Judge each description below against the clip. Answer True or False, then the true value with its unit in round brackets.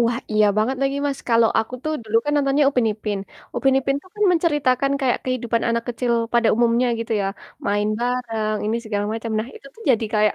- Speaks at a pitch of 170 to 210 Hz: False (235 Hz)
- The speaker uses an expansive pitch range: False (3.5 semitones)